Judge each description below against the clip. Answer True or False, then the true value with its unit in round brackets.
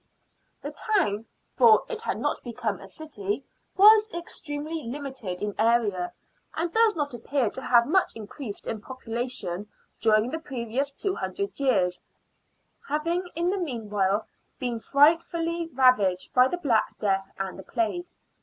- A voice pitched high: True (255 Hz)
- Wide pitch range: True (7.3 semitones)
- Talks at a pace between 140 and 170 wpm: True (150 wpm)